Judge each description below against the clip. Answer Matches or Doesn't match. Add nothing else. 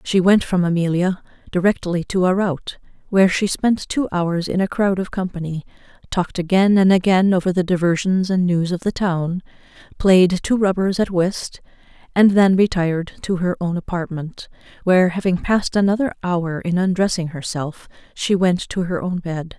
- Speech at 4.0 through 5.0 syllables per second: Matches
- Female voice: Matches